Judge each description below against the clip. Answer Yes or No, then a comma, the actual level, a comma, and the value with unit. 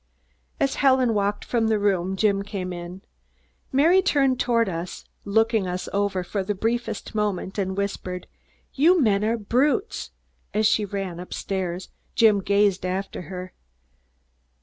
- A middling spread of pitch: Yes, average, 3.5 semitones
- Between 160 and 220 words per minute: No, average, 145 wpm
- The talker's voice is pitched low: No, high, 205 Hz